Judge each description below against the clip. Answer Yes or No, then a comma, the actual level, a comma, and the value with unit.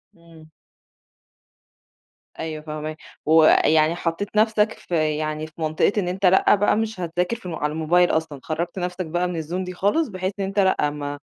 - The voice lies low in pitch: No, medium, 170 Hz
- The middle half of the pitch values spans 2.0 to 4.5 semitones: Yes, average, 3.1 semitones